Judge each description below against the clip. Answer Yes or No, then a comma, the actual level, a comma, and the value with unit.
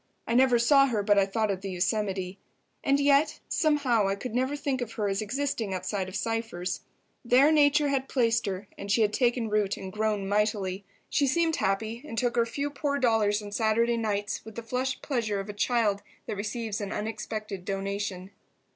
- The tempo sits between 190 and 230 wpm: Yes, average, 195 wpm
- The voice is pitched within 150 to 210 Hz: No, high, 220 Hz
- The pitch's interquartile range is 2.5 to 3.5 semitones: No, average, 4.0 semitones